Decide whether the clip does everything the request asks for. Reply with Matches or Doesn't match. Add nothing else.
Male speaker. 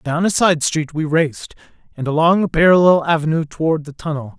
Matches